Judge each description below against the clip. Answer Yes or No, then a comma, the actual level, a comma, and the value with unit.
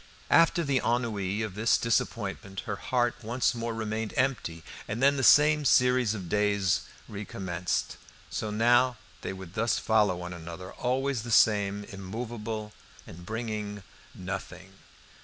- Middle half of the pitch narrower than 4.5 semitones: Yes, average, 3.7 semitones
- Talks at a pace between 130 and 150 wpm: Yes, average, 140 wpm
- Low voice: Yes, low, 110 Hz